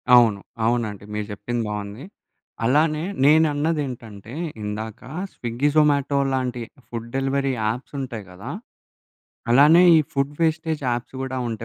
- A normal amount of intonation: Yes, average, 4.4 semitones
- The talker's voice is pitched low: Yes, low, 125 Hz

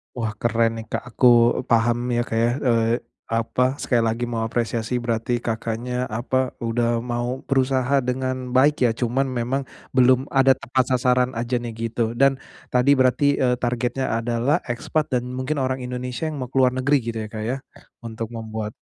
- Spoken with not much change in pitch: Yes, narrow, 2.0 semitones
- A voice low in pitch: Yes, low, 125 Hz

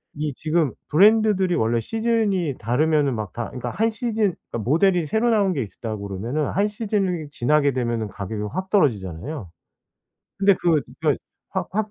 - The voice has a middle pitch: Yes, medium, 155 Hz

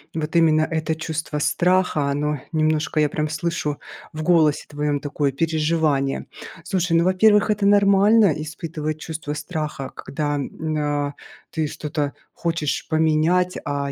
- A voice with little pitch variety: Yes, narrow, 2.1 semitones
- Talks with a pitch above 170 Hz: No, medium, 155 Hz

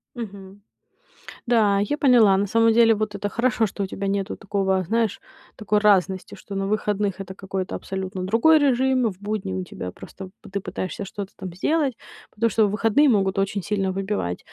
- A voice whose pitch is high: Yes, high, 205 Hz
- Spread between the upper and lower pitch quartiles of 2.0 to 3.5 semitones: Yes, average, 2.8 semitones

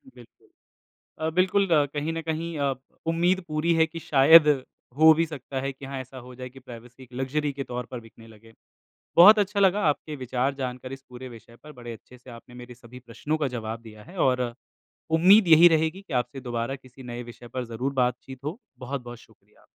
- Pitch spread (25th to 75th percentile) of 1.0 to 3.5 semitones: No, average, 4.5 semitones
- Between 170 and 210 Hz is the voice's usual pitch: No, low, 135 Hz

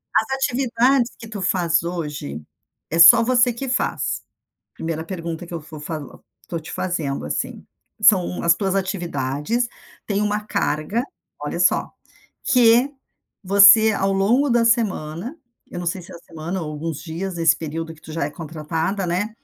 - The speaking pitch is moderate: Yes, medium, 180 Hz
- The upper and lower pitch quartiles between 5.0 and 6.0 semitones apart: Yes, average, 5.3 semitones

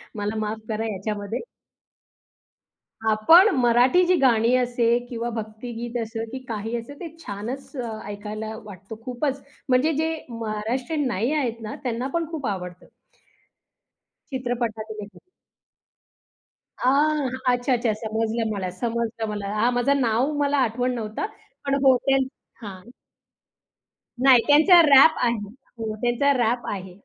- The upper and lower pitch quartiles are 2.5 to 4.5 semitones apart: Yes, average, 3.3 semitones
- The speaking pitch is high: Yes, high, 235 Hz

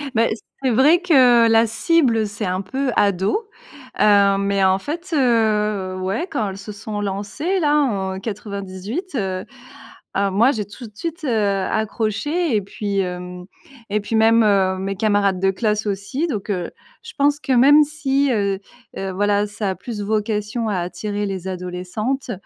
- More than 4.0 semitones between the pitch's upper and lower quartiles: Yes, average, 4.4 semitones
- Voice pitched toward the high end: Yes, high, 210 Hz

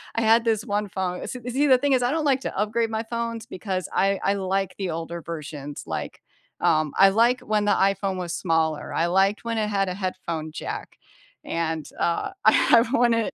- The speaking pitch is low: No, high, 195 Hz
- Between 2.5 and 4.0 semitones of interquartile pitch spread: No, average, 5.0 semitones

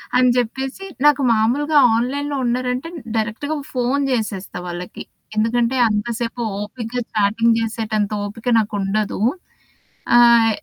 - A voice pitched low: No, high, 230 Hz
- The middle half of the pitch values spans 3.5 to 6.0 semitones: No, average, 2.7 semitones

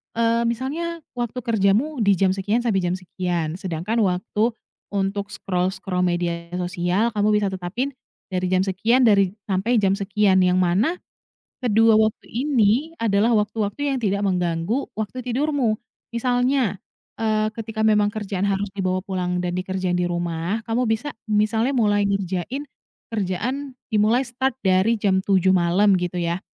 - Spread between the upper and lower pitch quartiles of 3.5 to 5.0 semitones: Yes, average, 3.9 semitones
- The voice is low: No, high, 205 Hz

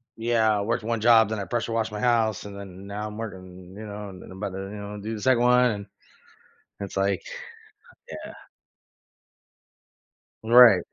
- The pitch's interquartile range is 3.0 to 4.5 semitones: No, narrow, 2.4 semitones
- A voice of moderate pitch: No, low, 105 Hz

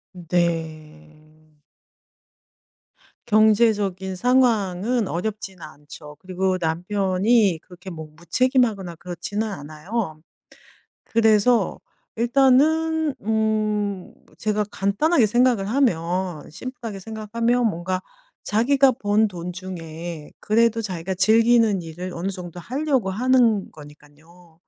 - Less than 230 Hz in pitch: Yes, high, 195 Hz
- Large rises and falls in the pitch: No, average, 4.9 semitones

